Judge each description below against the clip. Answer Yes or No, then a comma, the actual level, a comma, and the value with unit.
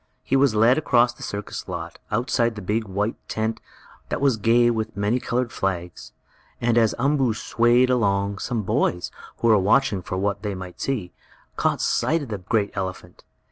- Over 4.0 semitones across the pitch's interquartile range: No, average, 3.3 semitones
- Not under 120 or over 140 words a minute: No, average, 180 wpm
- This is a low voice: Yes, low, 110 Hz